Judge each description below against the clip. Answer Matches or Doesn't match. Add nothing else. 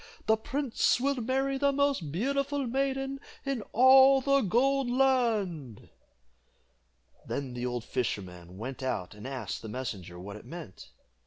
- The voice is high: Matches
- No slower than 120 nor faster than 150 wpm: Matches